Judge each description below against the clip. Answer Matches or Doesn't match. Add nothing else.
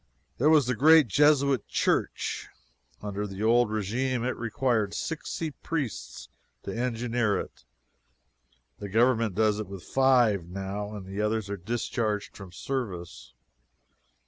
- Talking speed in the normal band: Doesn't match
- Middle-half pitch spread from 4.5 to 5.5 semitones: Doesn't match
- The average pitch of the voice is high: Doesn't match